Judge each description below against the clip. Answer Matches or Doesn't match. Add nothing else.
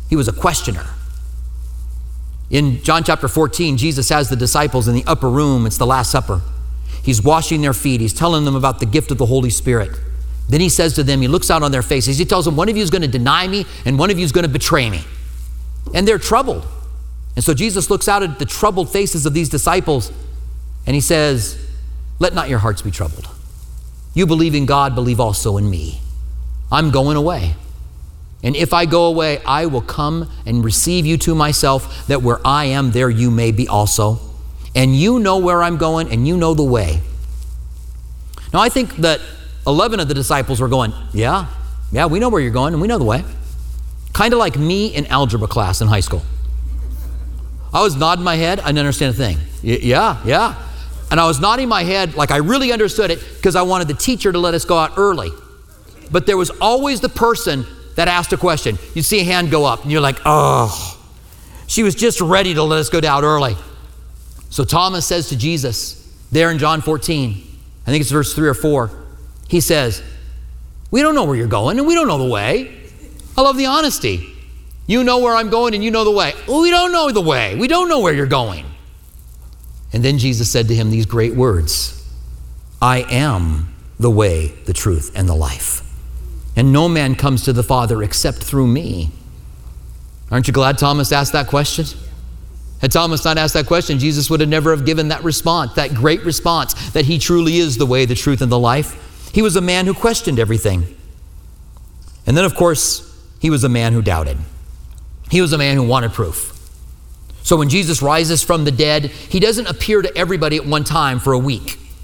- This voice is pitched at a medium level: Doesn't match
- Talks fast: Matches